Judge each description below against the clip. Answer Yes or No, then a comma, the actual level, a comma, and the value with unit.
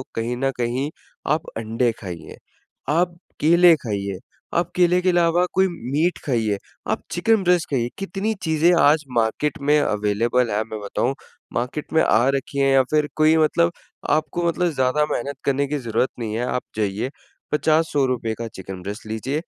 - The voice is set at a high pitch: No, medium, 140 Hz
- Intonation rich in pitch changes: Yes, wide, 5.9 semitones